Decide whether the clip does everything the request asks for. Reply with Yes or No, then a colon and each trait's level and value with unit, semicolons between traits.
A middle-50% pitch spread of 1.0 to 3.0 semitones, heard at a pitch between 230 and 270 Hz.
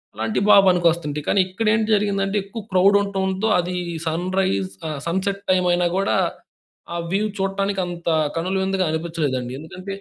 No: narrow, 2.6 semitones; medium, 185 Hz